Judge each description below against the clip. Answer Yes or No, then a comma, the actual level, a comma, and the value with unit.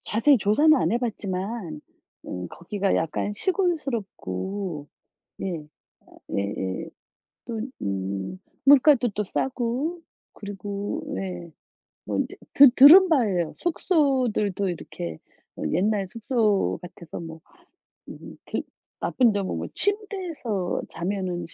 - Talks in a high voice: Yes, high, 205 Hz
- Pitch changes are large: Yes, wide, 6.9 semitones